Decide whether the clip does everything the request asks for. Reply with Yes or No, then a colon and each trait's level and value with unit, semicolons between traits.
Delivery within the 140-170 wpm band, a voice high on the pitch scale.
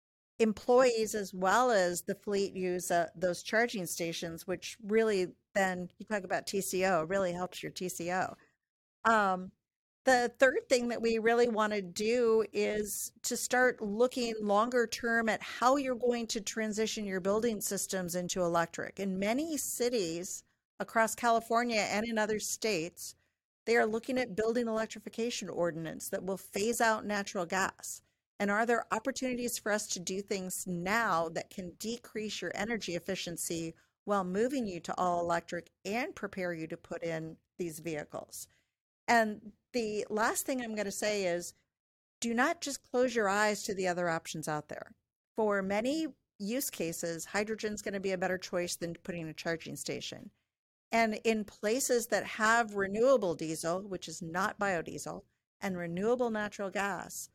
Yes: average, 160 wpm; high, 205 Hz